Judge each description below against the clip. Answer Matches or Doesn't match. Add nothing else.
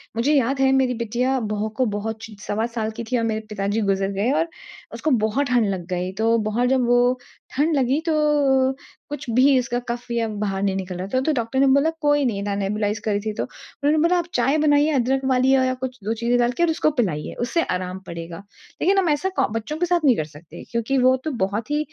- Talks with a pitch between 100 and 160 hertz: Doesn't match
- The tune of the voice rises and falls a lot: Doesn't match